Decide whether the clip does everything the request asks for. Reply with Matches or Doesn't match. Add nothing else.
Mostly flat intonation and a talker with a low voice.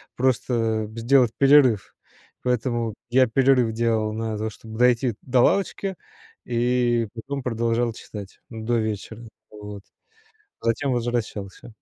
Matches